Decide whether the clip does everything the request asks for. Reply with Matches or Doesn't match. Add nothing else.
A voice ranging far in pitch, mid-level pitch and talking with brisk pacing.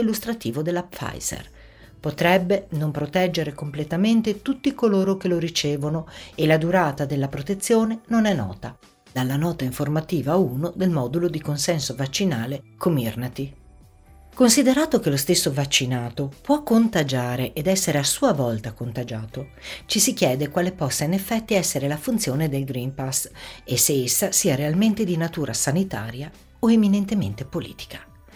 Doesn't match